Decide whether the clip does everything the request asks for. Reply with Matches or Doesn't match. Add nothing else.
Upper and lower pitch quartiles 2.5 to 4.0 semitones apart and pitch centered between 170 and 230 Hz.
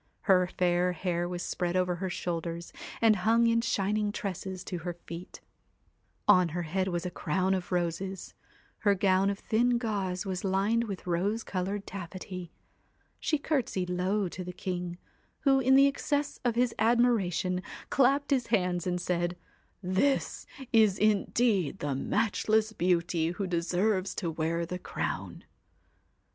Matches